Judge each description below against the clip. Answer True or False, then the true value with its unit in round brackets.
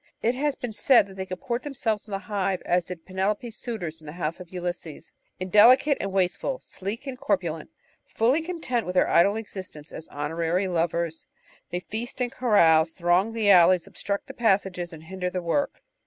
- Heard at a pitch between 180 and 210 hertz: True (190 Hz)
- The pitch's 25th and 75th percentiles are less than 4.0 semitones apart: False (4.6 semitones)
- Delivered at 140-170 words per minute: False (185 wpm)